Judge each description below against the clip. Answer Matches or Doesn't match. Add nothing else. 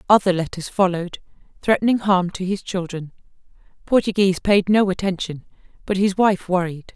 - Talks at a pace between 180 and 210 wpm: Doesn't match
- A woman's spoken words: Matches